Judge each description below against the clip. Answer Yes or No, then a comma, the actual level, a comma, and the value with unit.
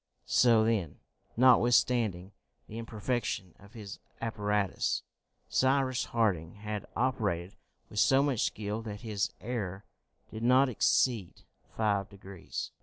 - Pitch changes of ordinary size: Yes, average, 3.3 semitones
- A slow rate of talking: Yes, slow, 110 wpm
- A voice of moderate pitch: No, low, 110 Hz